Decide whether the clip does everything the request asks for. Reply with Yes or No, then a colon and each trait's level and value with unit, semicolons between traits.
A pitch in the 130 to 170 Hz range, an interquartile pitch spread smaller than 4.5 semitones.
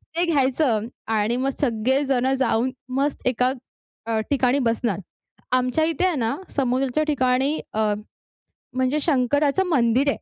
No: very high, 260 Hz; average, 2.8 semitones